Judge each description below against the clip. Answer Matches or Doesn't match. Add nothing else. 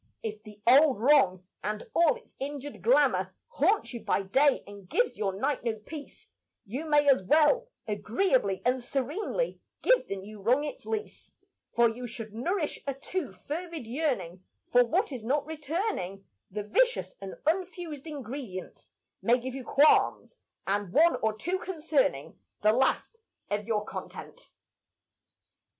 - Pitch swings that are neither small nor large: Doesn't match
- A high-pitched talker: Matches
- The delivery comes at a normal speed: Matches